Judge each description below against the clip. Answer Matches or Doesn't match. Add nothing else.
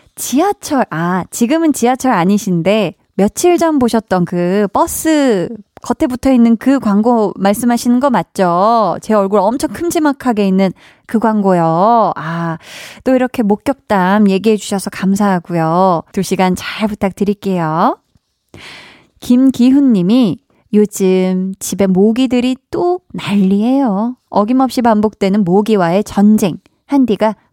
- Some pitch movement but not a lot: Matches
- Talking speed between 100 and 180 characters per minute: Doesn't match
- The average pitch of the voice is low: Doesn't match